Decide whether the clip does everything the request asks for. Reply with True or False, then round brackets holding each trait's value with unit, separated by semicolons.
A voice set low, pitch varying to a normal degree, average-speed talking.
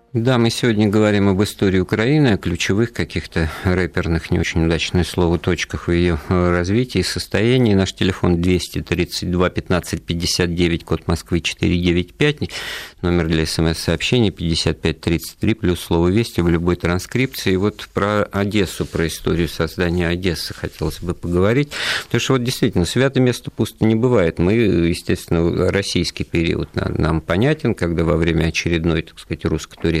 True (90 Hz; 3.9 semitones; 145 wpm)